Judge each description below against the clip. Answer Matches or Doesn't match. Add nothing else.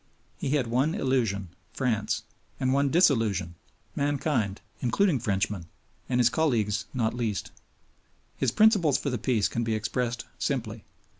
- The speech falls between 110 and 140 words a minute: Matches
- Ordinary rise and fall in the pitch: Matches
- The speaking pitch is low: Matches